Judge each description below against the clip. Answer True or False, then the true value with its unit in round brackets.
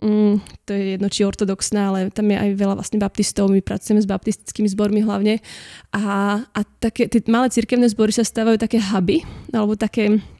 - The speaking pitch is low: False (210 Hz)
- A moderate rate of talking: False (180 wpm)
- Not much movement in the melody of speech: True (1.8 semitones)